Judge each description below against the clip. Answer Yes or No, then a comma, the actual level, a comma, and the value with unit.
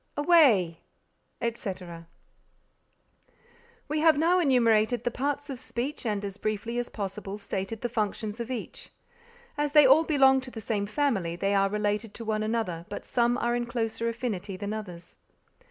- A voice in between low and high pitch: No, high, 225 Hz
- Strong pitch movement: No, average, 4.1 semitones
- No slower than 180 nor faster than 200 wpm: No, average, 160 wpm